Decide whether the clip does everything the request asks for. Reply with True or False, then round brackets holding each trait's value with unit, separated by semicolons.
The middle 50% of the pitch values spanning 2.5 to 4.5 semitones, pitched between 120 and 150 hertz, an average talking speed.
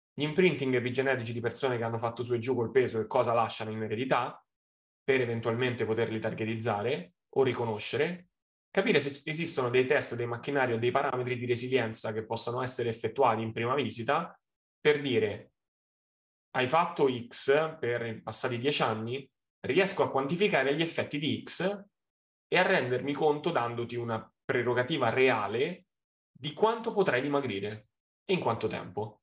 True (3.9 semitones; 125 Hz; 155 wpm)